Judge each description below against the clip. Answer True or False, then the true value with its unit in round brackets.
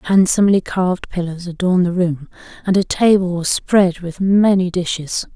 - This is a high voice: False (180 Hz)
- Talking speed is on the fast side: False (155 wpm)